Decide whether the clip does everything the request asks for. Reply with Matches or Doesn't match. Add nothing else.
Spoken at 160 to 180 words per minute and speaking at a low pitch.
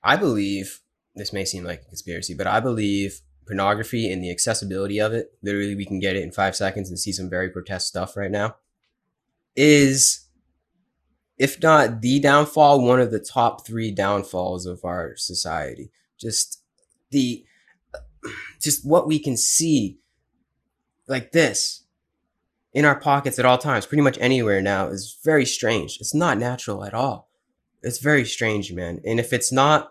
Matches